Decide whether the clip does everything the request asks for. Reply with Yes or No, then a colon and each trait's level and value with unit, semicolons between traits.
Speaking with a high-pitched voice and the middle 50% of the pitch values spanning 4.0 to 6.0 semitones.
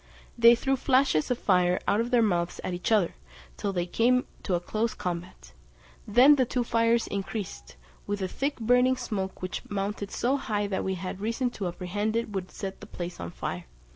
Yes: high, 205 Hz; average, 4.4 semitones